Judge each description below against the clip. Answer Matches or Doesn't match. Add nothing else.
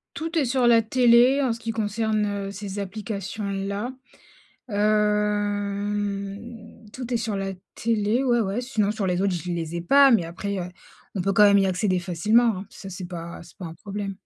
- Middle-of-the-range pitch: Doesn't match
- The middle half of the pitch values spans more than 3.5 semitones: Doesn't match